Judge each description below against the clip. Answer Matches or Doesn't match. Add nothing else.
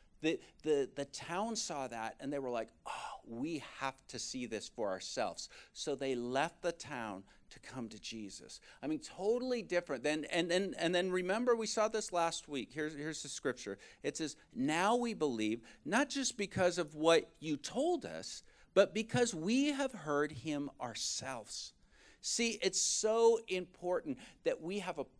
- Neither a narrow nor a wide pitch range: Doesn't match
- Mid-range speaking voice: Matches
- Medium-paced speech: Matches